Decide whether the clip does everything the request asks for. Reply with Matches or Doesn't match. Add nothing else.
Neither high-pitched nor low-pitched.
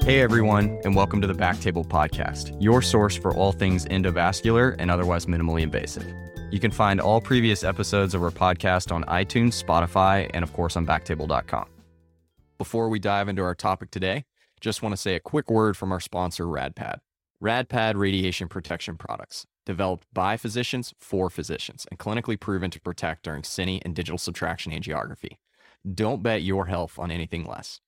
Doesn't match